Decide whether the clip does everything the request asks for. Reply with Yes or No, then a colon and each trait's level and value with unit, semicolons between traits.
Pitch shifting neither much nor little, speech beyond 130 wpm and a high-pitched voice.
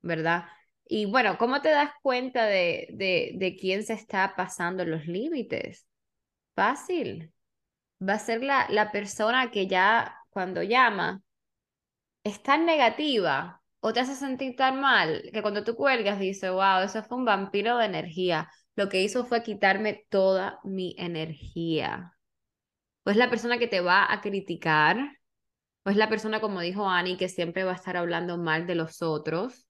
Yes: average, 5.0 semitones; average, 165 wpm; high, 200 Hz